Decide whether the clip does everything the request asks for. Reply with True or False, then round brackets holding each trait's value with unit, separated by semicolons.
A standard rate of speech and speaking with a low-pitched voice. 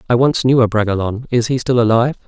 False (210 wpm; 120 Hz)